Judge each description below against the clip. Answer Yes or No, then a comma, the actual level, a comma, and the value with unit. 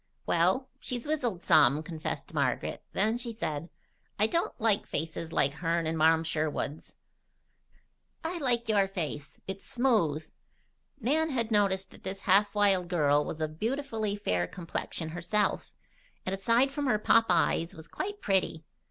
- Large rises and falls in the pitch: Yes, wide, 6.2 semitones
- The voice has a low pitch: No, high, 195 Hz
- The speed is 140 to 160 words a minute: Yes, average, 150 wpm